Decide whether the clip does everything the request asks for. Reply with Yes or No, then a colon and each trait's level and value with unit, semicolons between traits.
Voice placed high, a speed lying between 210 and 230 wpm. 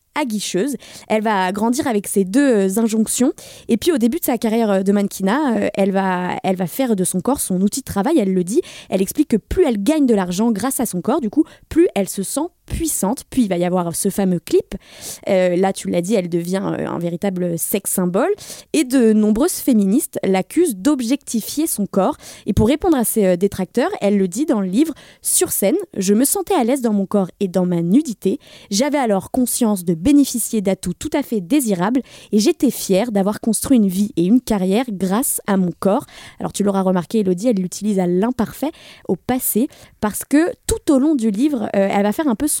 Yes: high, 215 Hz; average, 215 wpm